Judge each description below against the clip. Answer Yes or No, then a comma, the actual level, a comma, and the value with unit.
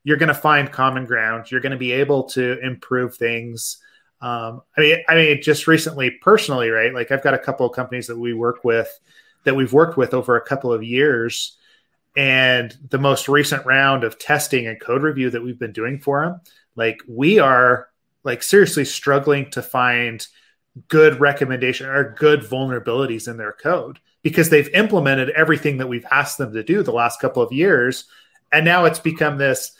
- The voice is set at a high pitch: No, low, 135 Hz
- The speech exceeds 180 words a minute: Yes, average, 190 wpm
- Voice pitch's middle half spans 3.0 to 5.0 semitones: Yes, average, 3.4 semitones